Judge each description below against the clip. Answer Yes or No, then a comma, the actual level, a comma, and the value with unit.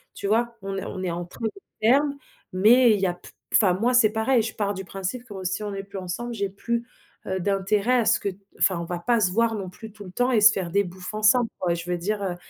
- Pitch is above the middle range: Yes, high, 205 Hz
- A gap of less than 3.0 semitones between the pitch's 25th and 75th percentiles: No, average, 3.6 semitones